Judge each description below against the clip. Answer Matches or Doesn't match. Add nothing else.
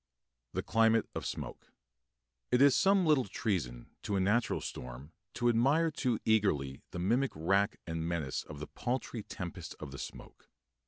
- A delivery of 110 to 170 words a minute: Matches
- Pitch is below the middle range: Matches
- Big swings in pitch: Matches